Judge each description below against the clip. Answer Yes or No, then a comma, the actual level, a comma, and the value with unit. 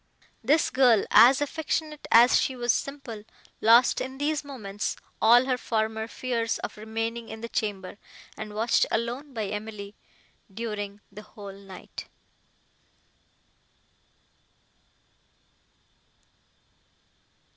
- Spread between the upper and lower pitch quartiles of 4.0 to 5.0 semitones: No, average, 3.4 semitones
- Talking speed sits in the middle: No, slow, 105 wpm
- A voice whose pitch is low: No, high, 230 Hz